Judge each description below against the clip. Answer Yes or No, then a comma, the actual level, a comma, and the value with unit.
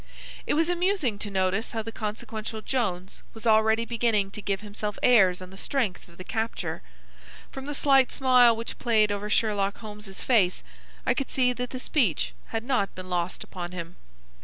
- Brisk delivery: No, average, 185 wpm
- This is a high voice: Yes, high, 220 Hz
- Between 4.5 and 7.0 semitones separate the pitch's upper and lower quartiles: No, average, 4.0 semitones